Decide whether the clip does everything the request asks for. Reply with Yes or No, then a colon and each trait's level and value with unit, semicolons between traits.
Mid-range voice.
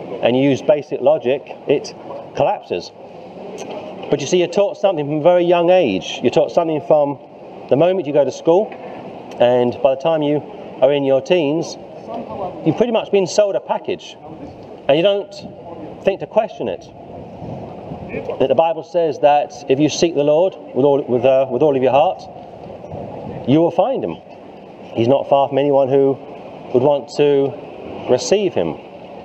Yes: medium, 150 Hz